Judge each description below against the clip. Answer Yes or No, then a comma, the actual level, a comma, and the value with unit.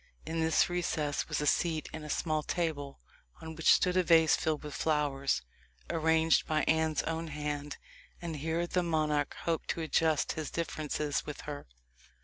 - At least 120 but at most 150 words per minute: No, average, 165 wpm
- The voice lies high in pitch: No, medium, 160 Hz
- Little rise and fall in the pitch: Yes, narrow, 1.6 semitones